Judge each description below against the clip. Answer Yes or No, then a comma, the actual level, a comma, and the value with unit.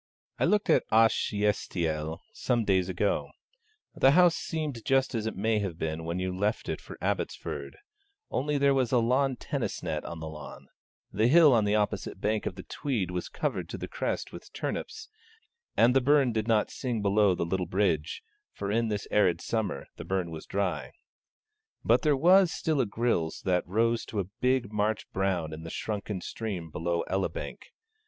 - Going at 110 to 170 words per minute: No, average, 185 wpm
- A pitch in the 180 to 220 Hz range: No, low, 105 Hz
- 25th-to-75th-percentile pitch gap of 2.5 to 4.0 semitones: No, wide, 5.4 semitones